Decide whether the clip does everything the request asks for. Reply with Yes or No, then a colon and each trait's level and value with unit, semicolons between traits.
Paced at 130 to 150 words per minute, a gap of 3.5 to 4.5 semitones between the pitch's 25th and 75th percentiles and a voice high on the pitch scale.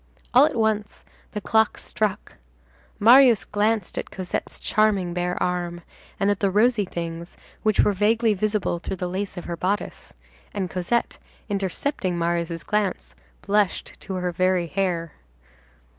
No: average, 145 wpm; average, 3.1 semitones; high, 195 Hz